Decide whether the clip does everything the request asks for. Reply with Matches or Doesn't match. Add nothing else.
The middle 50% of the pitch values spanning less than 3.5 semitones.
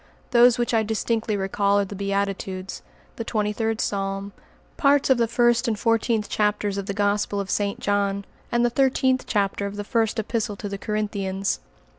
Matches